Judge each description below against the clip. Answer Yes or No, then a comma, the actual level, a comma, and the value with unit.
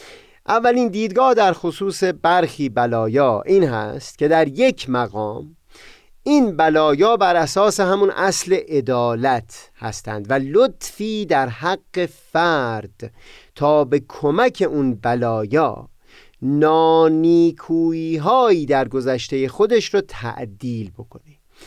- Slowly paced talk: Yes, slow, 100 wpm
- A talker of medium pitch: Yes, medium, 160 Hz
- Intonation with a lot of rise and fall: Yes, wide, 7.2 semitones